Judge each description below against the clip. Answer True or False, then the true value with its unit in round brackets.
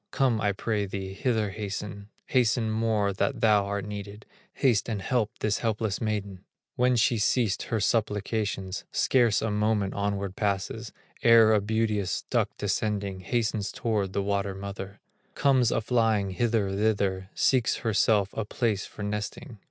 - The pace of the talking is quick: False (150 wpm)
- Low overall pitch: True (105 Hz)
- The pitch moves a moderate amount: False (2.1 semitones)